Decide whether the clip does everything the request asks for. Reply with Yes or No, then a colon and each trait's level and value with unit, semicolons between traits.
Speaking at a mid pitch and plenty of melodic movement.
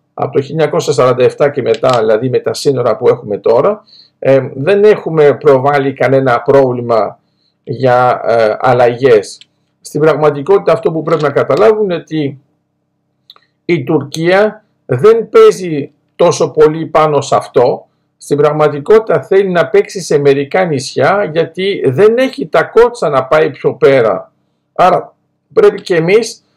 Yes: medium, 165 Hz; wide, 7.3 semitones